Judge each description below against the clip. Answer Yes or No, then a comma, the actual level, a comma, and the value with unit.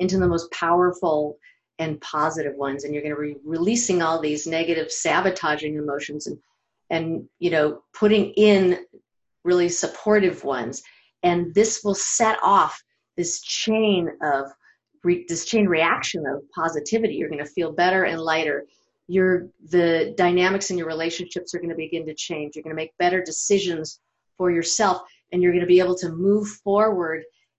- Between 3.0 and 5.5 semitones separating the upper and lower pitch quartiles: No, narrow, 2.6 semitones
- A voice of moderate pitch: Yes, medium, 175 Hz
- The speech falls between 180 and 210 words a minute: No, average, 165 wpm